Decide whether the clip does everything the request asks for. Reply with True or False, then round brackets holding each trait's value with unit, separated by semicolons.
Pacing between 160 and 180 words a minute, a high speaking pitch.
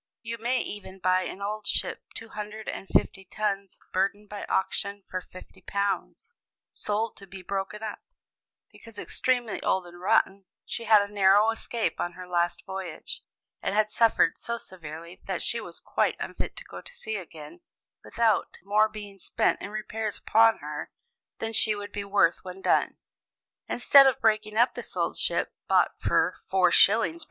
True (165 wpm; 205 Hz)